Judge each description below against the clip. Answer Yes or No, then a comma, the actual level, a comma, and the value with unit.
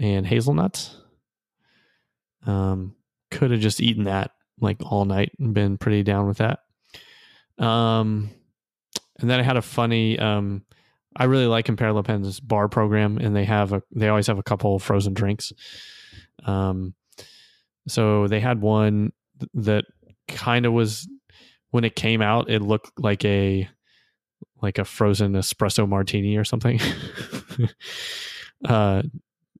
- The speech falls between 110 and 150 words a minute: Yes, average, 140 wpm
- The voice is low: Yes, low, 105 Hz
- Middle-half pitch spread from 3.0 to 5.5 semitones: No, narrow, 2.6 semitones